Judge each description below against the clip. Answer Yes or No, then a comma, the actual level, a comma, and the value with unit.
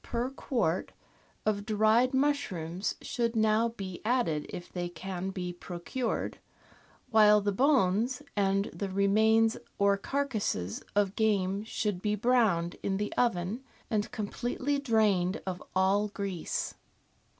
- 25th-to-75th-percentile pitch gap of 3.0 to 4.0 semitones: Yes, average, 3.5 semitones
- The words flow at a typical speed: No, slow, 130 wpm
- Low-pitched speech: No, high, 205 Hz